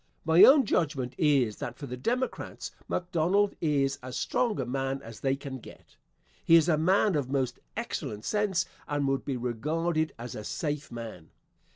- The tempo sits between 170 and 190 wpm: Yes, average, 175 wpm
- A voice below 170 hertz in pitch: Yes, medium, 140 Hz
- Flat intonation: No, average, 5.0 semitones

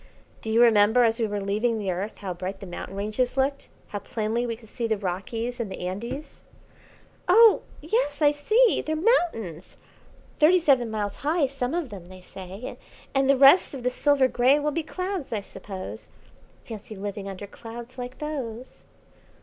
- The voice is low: No, high, 235 Hz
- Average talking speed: Yes, average, 180 wpm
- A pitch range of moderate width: No, wide, 5.8 semitones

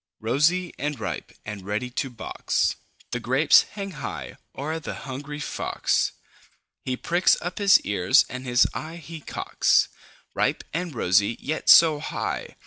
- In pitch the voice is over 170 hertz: No, medium, 145 Hz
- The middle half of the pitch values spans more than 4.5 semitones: Yes, average, 4.9 semitones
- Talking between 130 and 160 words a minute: Yes, average, 145 wpm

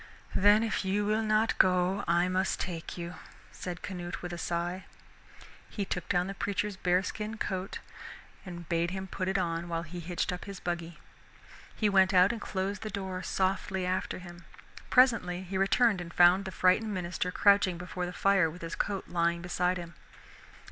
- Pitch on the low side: No, medium, 185 Hz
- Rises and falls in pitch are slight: Yes, narrow, 2.1 semitones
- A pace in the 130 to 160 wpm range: No, average, 180 wpm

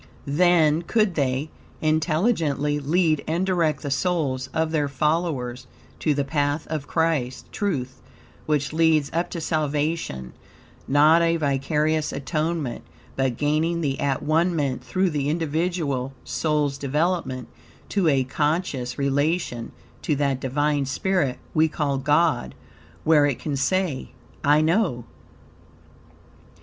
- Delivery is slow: Yes, slow, 125 wpm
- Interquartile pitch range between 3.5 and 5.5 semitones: No, average, 3.1 semitones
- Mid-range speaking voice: Yes, medium, 150 Hz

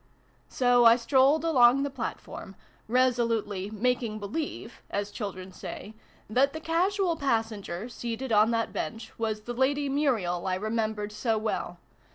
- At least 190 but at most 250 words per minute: No, average, 155 wpm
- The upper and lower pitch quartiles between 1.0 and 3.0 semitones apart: No, average, 3.8 semitones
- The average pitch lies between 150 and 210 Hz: No, high, 230 Hz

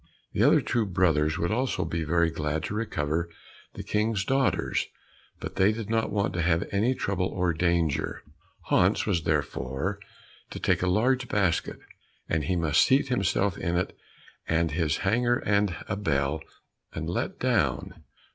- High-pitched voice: No, very low, 90 Hz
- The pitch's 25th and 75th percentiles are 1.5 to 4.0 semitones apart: No, average, 4.4 semitones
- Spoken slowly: No, average, 165 wpm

